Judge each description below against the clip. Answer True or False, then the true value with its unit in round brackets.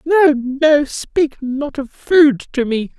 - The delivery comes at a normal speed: True (160 wpm)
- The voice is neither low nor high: False (280 Hz)